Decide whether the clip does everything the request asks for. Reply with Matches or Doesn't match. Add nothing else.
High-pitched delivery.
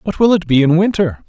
Doesn't match